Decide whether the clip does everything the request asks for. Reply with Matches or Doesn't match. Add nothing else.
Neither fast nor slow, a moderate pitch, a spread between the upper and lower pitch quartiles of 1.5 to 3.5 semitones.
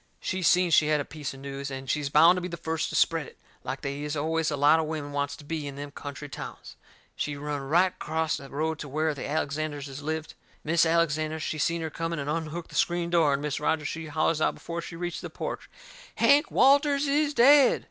Doesn't match